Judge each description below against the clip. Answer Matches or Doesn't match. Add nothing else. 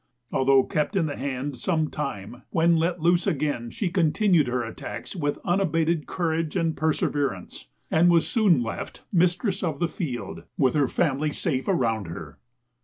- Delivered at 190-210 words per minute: Doesn't match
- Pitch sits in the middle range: Matches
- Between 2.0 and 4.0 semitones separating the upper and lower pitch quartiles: Doesn't match